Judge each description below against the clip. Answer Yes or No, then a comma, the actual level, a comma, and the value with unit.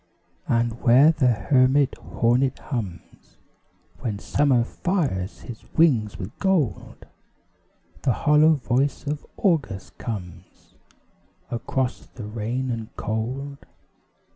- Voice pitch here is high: No, low, 125 Hz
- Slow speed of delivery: Yes, slow, 100 wpm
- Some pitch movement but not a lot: Yes, average, 4.2 semitones